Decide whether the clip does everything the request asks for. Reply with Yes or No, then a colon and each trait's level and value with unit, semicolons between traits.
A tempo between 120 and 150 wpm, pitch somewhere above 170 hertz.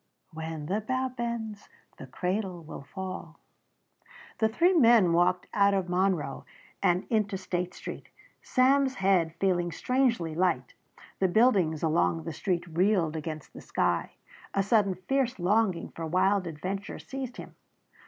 Yes: average, 140 wpm; medium, 185 Hz